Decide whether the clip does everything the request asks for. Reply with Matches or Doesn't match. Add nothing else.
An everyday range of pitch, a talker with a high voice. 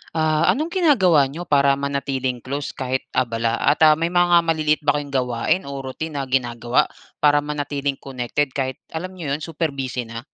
Doesn't match